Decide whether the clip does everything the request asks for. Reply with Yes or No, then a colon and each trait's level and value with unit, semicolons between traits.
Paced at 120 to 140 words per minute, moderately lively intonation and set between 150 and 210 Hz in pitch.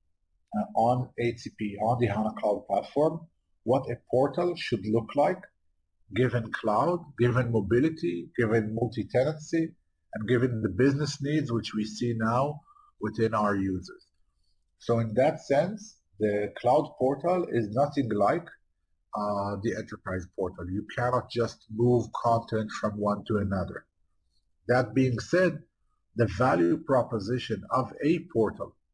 No: slow, 135 wpm; average, 4.3 semitones; low, 115 Hz